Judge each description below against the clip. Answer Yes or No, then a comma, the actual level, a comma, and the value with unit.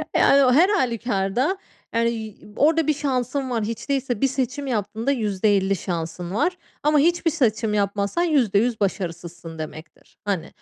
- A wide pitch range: Yes, wide, 5.8 semitones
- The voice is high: Yes, high, 230 Hz